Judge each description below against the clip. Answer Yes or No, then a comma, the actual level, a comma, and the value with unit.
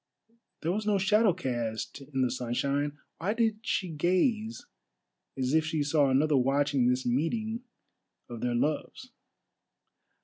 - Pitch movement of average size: No, wide, 7.4 semitones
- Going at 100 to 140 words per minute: Yes, slow, 135 wpm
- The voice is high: No, medium, 150 Hz